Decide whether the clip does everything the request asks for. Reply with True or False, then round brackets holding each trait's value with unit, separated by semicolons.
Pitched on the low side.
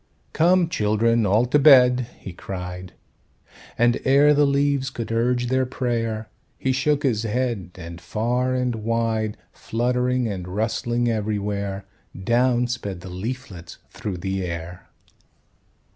True (115 Hz)